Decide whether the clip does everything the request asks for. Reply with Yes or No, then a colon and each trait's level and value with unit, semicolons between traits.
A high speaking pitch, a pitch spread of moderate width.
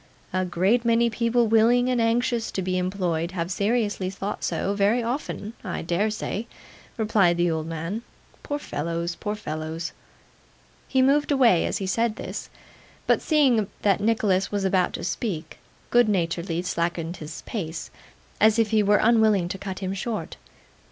Yes: high, 200 Hz; average, 4.6 semitones